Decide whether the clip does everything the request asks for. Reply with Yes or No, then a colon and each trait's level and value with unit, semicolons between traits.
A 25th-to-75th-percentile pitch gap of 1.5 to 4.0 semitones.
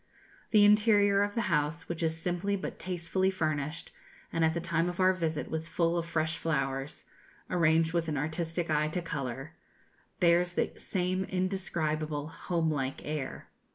Yes: average, 2.7 semitones